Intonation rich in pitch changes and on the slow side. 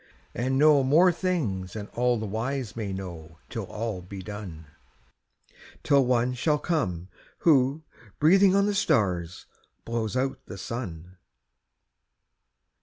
Yes: wide, 6.9 semitones; slow, 125 wpm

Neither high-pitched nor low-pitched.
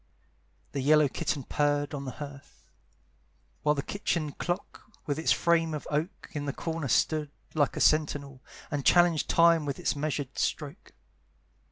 Yes: medium, 150 Hz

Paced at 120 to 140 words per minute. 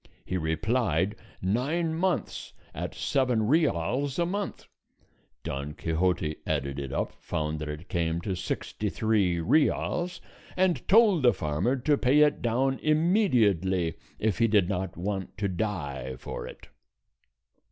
Yes: slow, 135 wpm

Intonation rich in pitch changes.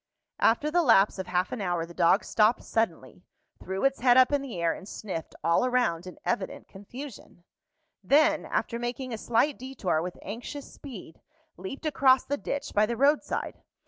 Yes: wide, 6.4 semitones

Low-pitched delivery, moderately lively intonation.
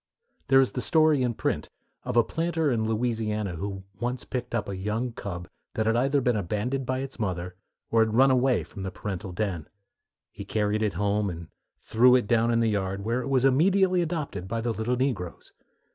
Yes: low, 115 Hz; average, 4.1 semitones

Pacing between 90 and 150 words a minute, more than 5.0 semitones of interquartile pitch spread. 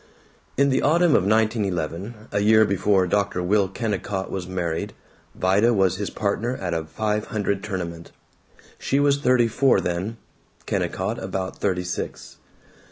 No: average, 145 wpm; average, 3.3 semitones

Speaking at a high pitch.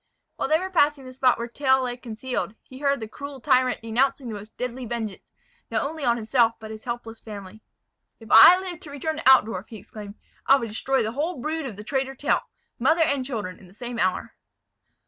Yes: very high, 250 Hz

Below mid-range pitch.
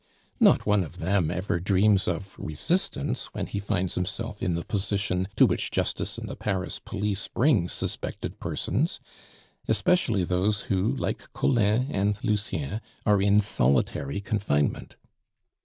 Yes: low, 100 Hz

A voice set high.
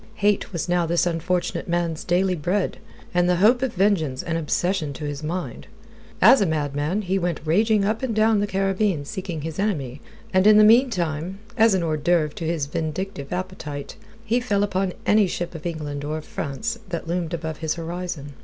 No: medium, 175 Hz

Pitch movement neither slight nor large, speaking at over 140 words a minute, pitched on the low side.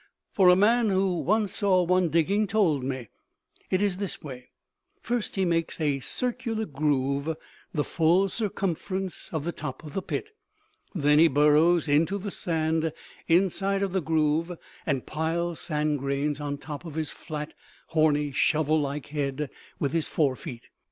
No: average, 4.2 semitones; average, 160 wpm; medium, 160 Hz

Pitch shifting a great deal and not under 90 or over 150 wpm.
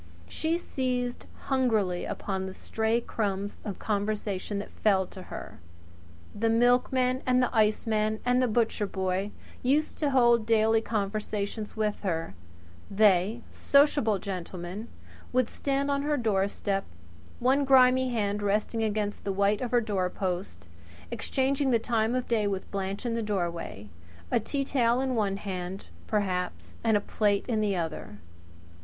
No: average, 3.8 semitones; average, 145 wpm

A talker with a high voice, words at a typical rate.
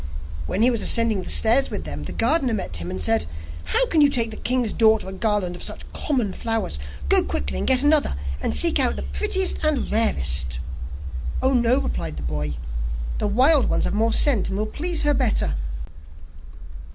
Yes: high, 220 Hz; average, 195 wpm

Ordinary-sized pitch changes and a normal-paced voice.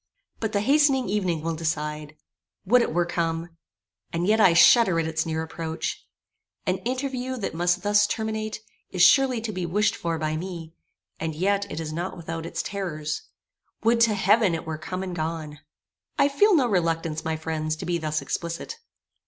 Yes: average, 4.9 semitones; average, 180 wpm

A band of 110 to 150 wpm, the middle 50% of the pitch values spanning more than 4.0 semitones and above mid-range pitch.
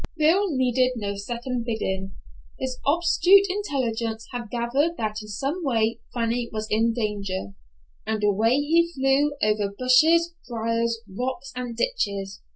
Yes: slow, 135 wpm; average, 4.5 semitones; high, 240 Hz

